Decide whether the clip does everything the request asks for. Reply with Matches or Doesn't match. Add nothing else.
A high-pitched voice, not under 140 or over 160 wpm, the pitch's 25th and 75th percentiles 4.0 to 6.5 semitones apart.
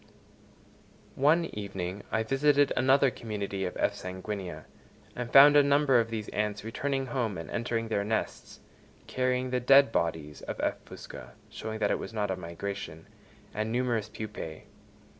Doesn't match